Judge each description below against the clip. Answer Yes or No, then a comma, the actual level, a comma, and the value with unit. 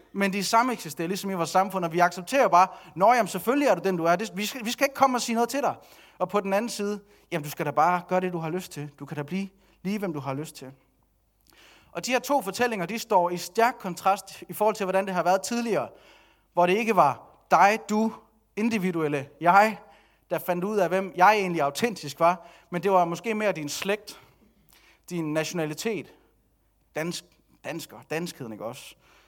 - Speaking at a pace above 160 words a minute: Yes, average, 215 wpm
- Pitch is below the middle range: No, medium, 185 Hz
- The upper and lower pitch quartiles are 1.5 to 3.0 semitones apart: No, average, 3.9 semitones